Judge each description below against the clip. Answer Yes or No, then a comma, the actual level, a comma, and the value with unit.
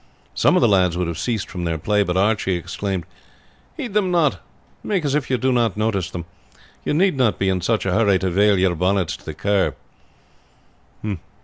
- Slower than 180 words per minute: No, fast, 205 wpm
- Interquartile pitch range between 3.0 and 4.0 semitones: No, average, 4.8 semitones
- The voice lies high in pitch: No, low, 100 Hz